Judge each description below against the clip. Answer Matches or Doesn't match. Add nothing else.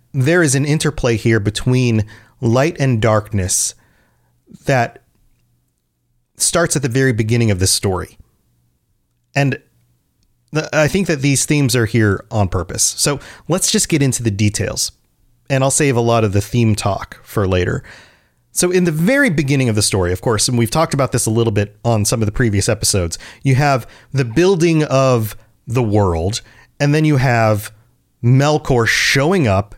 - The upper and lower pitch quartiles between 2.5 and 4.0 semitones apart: Doesn't match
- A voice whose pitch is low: Matches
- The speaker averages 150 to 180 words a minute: Matches